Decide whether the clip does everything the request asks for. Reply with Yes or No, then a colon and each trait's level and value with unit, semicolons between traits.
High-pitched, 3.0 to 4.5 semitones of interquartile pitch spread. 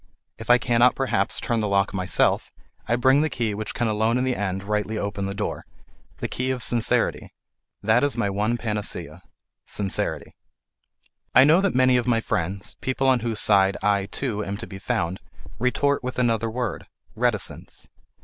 No: low, 115 Hz; average, 3.6 semitones